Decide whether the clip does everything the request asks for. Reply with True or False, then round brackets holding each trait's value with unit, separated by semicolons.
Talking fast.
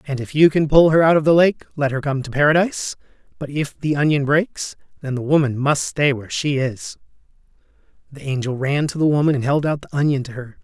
True (230 wpm)